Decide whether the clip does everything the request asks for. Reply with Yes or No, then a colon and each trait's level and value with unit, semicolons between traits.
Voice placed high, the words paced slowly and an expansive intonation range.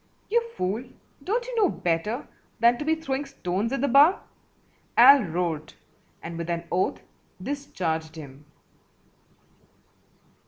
Yes: high, 220 Hz; slow, 125 wpm; wide, 9.0 semitones